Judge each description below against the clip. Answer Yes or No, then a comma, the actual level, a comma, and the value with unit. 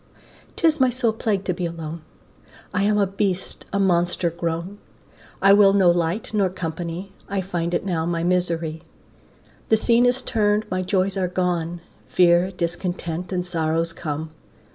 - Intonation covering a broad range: No, average, 2.8 semitones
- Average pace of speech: Yes, average, 160 wpm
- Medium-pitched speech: Yes, medium, 180 Hz